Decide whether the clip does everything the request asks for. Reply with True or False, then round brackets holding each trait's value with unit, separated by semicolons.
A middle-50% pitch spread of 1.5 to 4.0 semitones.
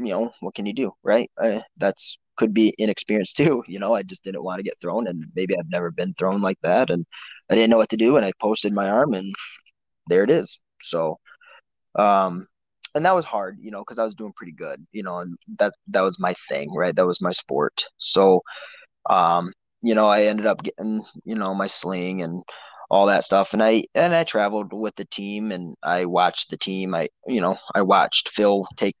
True (2.7 semitones)